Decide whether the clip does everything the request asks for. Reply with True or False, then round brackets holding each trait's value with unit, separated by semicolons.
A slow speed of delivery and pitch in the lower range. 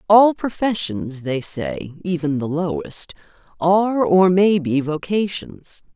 False (120 wpm; 180 Hz)